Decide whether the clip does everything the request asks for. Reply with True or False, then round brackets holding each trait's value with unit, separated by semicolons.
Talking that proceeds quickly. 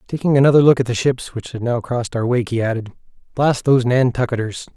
True (215 wpm)